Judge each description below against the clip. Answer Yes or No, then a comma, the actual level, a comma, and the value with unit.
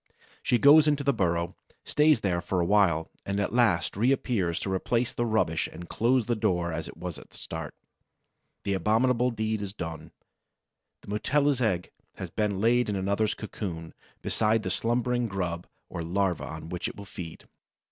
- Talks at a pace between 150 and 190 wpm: Yes, average, 180 wpm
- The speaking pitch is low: Yes, low, 100 Hz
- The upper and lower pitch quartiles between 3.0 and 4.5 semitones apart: No, average, 5.3 semitones